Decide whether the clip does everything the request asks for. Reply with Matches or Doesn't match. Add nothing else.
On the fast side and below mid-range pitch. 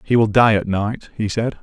Matches